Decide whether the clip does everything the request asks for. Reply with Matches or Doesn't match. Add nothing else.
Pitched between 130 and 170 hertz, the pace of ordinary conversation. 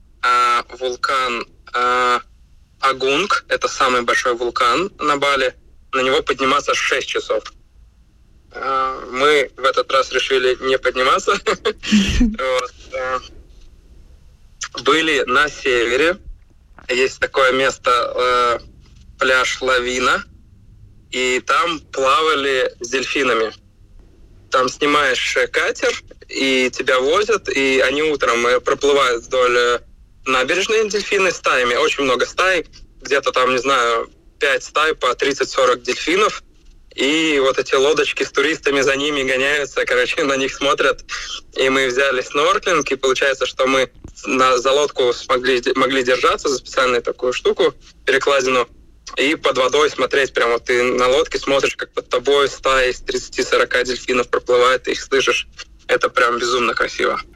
Matches